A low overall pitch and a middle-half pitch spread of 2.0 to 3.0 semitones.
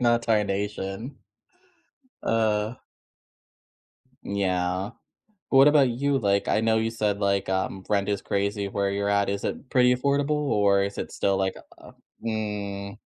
Yes: low, 105 Hz; narrow, 2.6 semitones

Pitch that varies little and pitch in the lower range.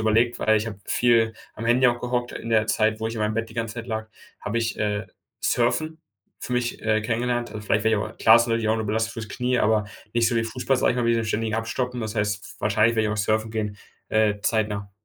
Yes: narrow, 1.6 semitones; low, 110 Hz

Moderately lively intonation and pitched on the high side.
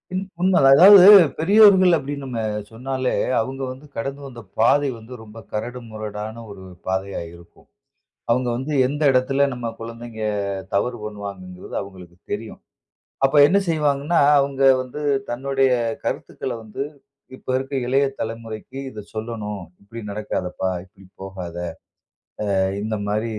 No: average, 4.4 semitones; low, 120 Hz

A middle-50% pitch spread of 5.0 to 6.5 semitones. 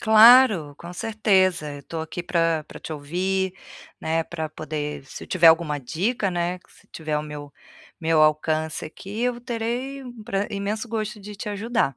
Yes: wide, 5.5 semitones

